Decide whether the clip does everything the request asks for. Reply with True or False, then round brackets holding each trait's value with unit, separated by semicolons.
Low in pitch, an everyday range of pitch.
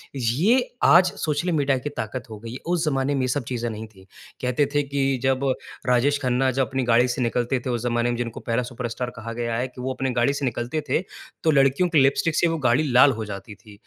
True (125 Hz; 3.0 semitones)